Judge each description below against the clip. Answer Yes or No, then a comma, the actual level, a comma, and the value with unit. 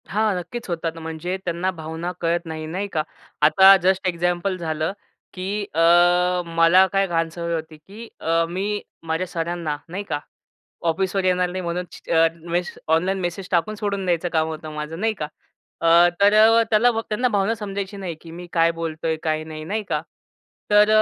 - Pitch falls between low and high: Yes, medium, 175 Hz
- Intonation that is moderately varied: Yes, average, 3.0 semitones